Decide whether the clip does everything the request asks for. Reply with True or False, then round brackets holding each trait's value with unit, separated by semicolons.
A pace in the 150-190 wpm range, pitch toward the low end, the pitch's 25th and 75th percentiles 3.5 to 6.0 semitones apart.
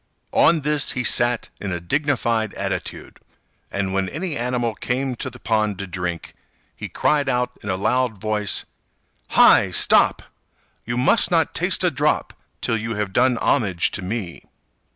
True (160 wpm; 115 Hz; 4.3 semitones)